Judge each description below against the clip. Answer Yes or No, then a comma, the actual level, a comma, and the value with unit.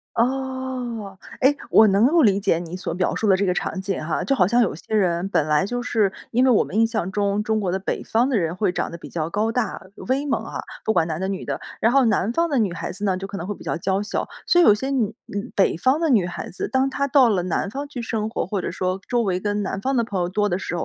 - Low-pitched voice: No, high, 210 Hz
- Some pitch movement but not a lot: Yes, average, 4.6 semitones